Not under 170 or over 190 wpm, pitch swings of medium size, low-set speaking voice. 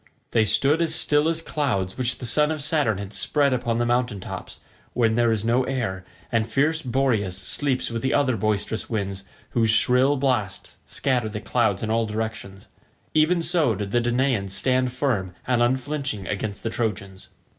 Yes: average, 175 wpm; average, 4.3 semitones; low, 120 Hz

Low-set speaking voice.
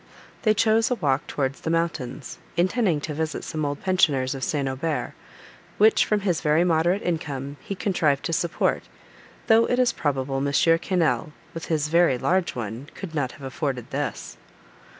No: medium, 160 Hz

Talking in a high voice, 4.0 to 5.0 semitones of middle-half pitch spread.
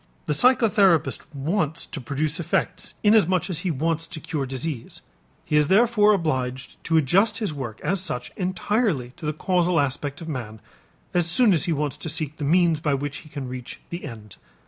No: medium, 155 Hz; average, 4.5 semitones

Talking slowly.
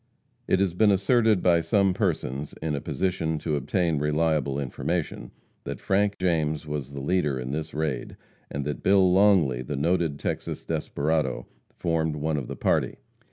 No: average, 160 wpm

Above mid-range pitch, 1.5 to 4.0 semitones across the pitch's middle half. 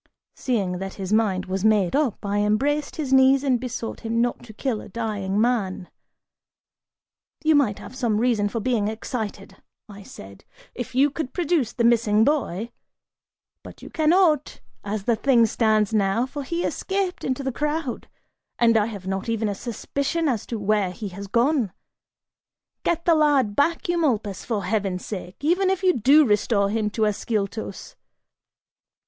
No: high, 230 Hz; average, 5.2 semitones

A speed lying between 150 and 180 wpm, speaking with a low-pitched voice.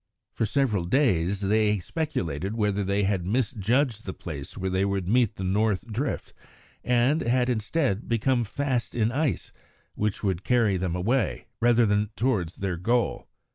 Yes: average, 155 wpm; low, 105 Hz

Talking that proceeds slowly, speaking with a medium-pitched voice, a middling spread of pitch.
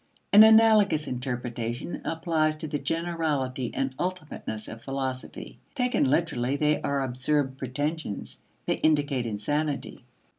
Yes: slow, 115 wpm; medium, 145 Hz; average, 3.9 semitones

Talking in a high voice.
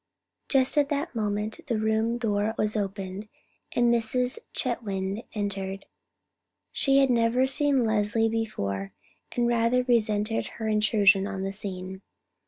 Yes: high, 220 Hz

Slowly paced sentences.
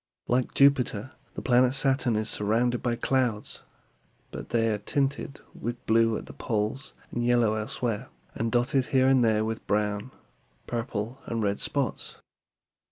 No: average, 145 wpm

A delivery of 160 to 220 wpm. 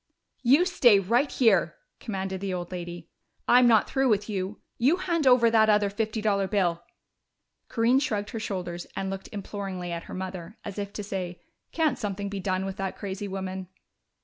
Yes: average, 180 wpm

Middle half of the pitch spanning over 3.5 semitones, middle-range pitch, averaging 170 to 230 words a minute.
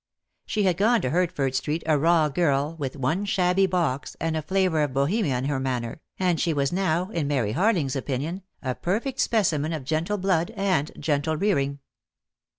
Yes: average, 4.6 semitones; medium, 160 Hz; average, 185 wpm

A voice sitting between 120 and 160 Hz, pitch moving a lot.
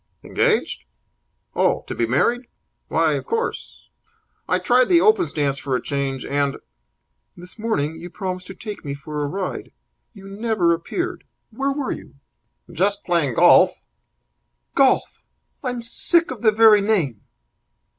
No: high, 195 Hz; wide, 8.6 semitones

